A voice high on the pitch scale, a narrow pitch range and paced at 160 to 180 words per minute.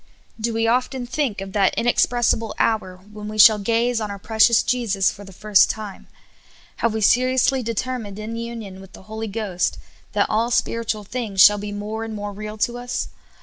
No: high, 220 Hz; narrow, 2.3 semitones; average, 190 wpm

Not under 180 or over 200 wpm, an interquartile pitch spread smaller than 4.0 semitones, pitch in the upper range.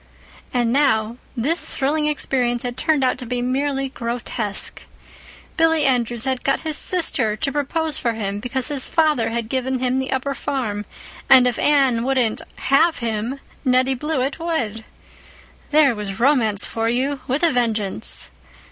No: average, 155 wpm; average, 3.4 semitones; very high, 255 Hz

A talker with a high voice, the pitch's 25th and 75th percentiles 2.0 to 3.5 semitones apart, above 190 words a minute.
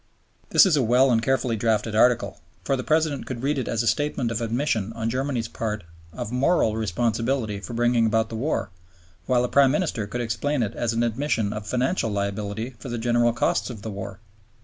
No: low, 115 Hz; average, 2.9 semitones; average, 200 wpm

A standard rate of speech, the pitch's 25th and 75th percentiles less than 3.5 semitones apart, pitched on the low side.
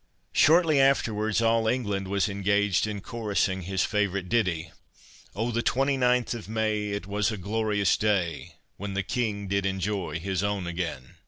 Yes: average, 160 wpm; average, 2.8 semitones; low, 105 Hz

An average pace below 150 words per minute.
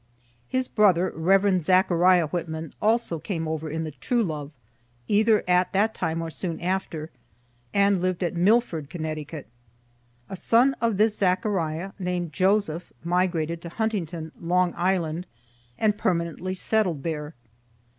Yes: slow, 135 wpm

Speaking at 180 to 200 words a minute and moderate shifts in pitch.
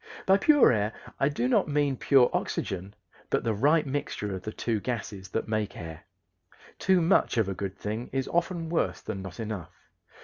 No: average, 190 wpm; wide, 6.5 semitones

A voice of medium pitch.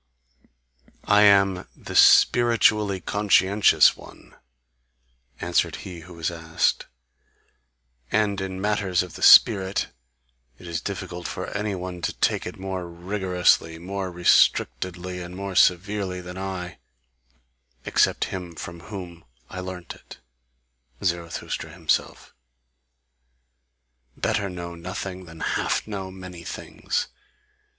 No: very low, 90 Hz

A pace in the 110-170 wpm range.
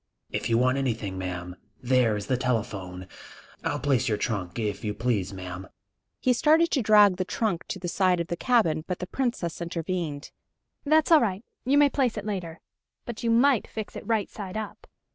No: average, 195 wpm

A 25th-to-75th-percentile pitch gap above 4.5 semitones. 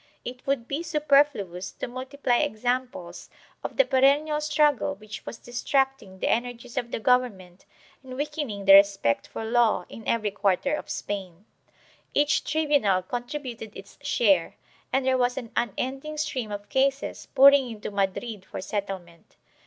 Yes: wide, 5.4 semitones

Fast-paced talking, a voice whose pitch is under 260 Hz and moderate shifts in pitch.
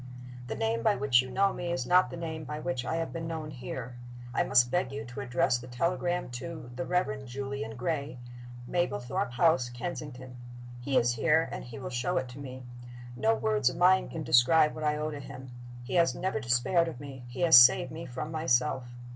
Yes: fast, 210 wpm; low, 135 Hz; average, 4.9 semitones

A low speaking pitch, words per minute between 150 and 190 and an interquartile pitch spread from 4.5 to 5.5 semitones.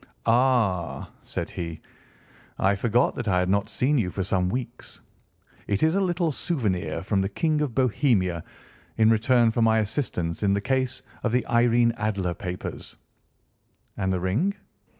Yes: low, 110 Hz; average, 160 wpm; average, 5.1 semitones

